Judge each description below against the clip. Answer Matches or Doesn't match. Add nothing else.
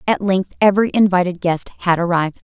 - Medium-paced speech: Matches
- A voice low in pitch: Doesn't match